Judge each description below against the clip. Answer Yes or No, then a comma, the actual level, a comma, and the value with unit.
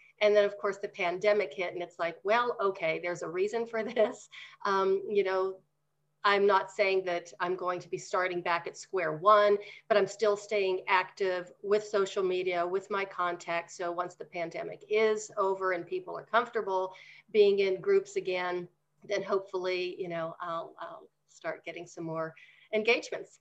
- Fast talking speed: No, average, 175 wpm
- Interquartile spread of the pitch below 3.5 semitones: Yes, average, 2.8 semitones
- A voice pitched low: No, high, 190 Hz